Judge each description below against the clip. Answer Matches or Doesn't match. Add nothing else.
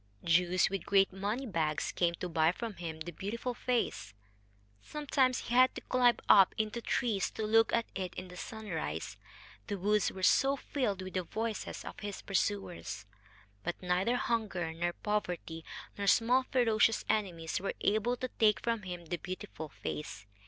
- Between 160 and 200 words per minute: Matches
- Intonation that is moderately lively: Matches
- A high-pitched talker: Matches